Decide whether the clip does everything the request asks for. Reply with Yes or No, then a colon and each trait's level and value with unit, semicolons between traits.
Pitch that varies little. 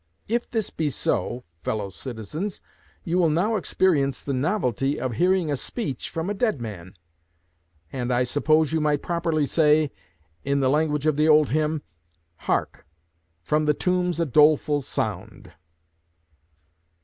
No: average, 3.9 semitones